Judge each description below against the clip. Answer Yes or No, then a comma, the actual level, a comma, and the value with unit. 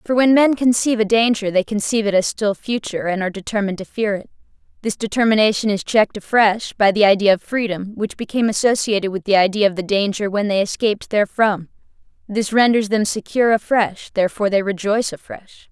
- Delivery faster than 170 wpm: Yes, average, 190 wpm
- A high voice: Yes, high, 210 Hz